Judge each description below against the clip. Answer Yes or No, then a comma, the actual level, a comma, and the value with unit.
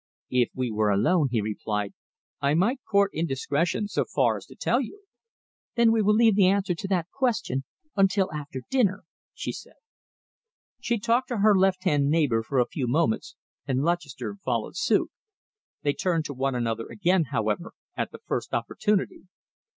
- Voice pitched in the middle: Yes, medium, 165 Hz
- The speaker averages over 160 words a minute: Yes, average, 170 wpm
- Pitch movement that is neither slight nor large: No, wide, 7.7 semitones